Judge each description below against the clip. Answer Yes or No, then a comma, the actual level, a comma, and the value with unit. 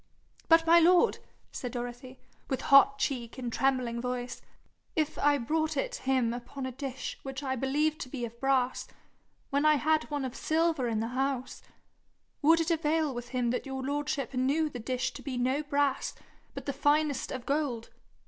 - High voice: Yes, very high, 270 Hz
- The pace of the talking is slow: No, average, 180 wpm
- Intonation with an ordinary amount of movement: Yes, average, 3.1 semitones